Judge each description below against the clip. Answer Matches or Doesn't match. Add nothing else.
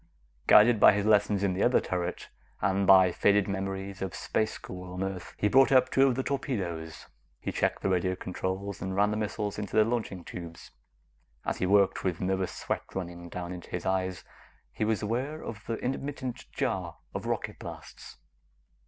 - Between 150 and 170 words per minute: Doesn't match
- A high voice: Doesn't match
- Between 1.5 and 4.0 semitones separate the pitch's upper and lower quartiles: Matches